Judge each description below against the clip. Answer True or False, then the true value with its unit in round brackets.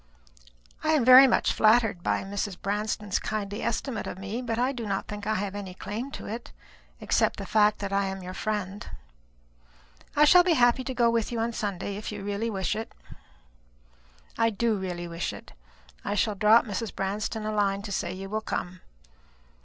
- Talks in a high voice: True (210 Hz)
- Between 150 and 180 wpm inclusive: False (190 wpm)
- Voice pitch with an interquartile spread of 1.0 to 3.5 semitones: True (2.8 semitones)